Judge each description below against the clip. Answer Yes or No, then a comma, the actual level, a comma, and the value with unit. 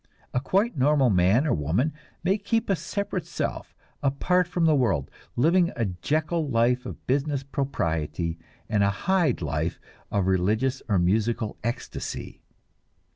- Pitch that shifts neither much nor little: No, wide, 7.9 semitones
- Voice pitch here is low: Yes, low, 130 Hz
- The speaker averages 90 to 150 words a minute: Yes, average, 140 wpm